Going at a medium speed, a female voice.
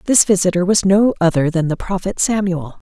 Yes: average, 190 wpm; female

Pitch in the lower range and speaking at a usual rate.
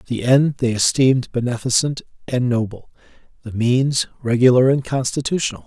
No: low, 125 Hz; slow, 125 wpm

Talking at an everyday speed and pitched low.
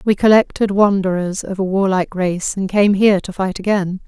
No: average, 190 wpm; high, 195 Hz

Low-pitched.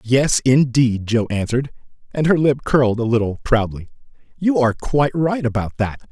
Yes: low, 125 Hz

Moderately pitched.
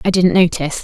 Yes: medium, 175 Hz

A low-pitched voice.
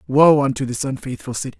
Yes: low, 130 Hz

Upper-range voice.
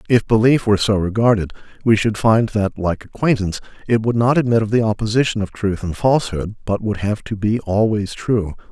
No: low, 110 Hz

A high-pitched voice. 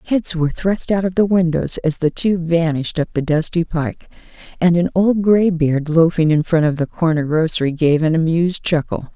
No: medium, 165 Hz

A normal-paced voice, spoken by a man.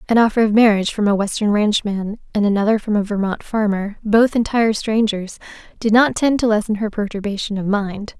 No: average, 190 wpm; female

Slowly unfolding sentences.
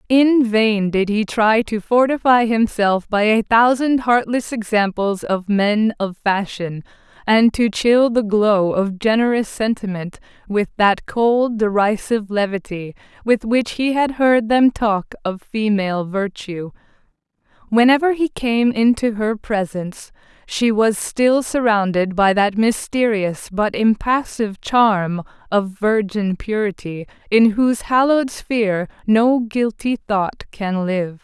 Yes: slow, 130 wpm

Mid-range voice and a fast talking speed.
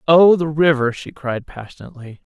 No: medium, 145 Hz; average, 155 wpm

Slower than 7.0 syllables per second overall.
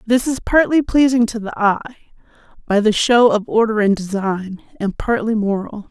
Yes: 4.9 syllables/s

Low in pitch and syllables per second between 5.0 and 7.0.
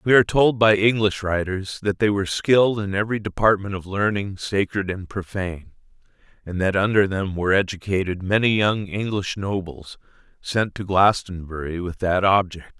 Yes: low, 100 Hz; 5.1 syllables/s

